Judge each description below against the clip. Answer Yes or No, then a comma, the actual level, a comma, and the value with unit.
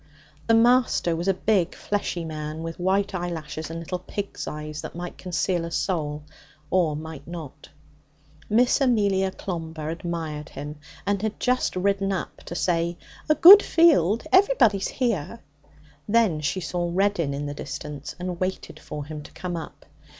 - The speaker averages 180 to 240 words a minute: No, average, 155 wpm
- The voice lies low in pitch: No, medium, 175 Hz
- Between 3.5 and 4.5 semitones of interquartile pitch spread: Yes, average, 4.2 semitones